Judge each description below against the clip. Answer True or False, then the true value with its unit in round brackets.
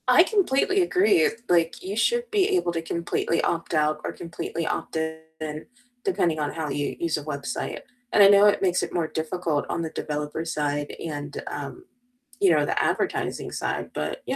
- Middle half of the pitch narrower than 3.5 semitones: False (4.2 semitones)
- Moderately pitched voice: True (165 Hz)